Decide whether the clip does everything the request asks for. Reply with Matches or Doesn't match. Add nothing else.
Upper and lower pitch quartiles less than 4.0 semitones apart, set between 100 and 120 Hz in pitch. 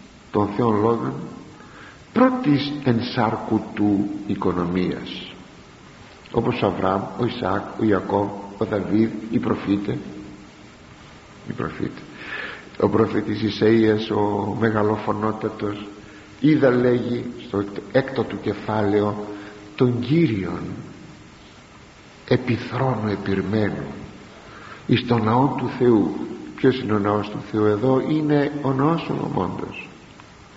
Matches